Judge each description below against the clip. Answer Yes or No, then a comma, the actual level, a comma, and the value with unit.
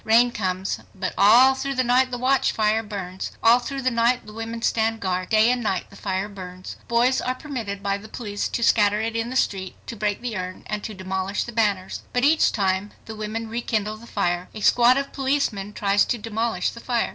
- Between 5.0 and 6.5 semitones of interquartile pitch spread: No, average, 3.4 semitones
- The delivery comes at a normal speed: No, fast, 215 wpm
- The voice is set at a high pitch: Yes, high, 220 Hz